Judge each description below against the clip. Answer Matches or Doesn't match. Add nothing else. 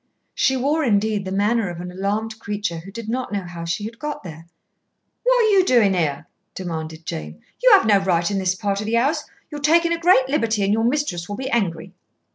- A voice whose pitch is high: Matches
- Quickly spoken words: Matches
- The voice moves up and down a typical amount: Doesn't match